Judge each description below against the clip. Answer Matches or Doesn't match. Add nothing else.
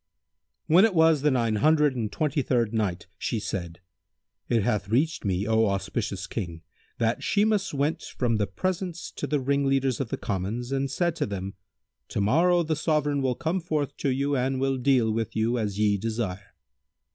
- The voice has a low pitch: Matches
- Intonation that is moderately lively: Doesn't match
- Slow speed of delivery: Doesn't match